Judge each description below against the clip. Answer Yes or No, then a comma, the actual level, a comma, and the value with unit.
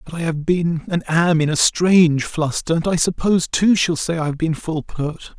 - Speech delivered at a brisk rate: Yes, fast, 235 wpm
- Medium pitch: Yes, medium, 165 Hz